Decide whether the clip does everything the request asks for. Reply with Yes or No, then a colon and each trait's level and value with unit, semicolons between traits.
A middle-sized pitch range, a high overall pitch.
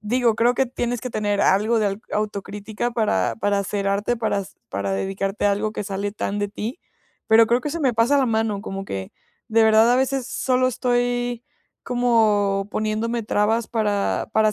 Yes: average, 3.0 semitones; high, 220 Hz